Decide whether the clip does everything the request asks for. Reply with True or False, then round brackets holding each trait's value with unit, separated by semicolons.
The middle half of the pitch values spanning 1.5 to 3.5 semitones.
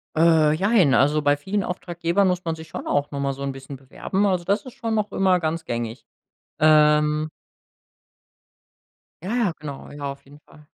False (4.2 semitones)